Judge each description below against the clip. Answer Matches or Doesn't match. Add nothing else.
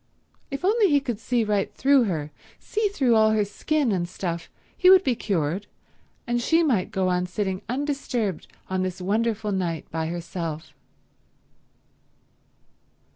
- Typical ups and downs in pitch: Doesn't match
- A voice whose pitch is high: Matches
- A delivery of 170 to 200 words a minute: Doesn't match